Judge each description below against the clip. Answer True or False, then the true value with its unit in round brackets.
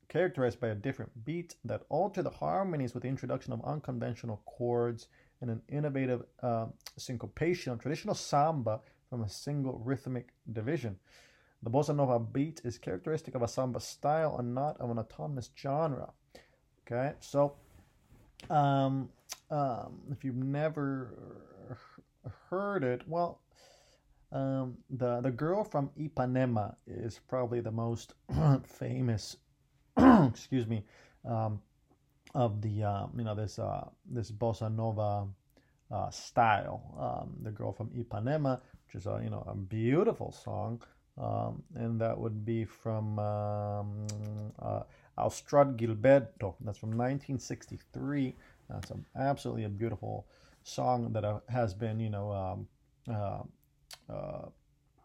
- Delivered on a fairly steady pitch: False (3.3 semitones)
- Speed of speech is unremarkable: False (130 wpm)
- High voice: False (125 Hz)